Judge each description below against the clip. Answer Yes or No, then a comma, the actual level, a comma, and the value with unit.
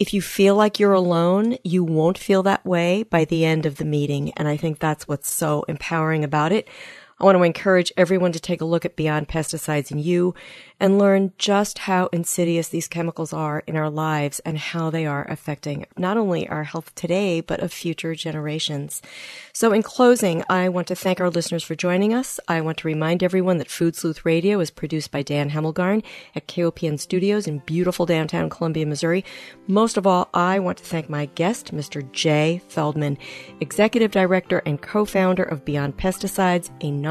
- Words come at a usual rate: Yes, average, 190 wpm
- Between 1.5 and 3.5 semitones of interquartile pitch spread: Yes, average, 3.1 semitones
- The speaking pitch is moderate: Yes, medium, 170 Hz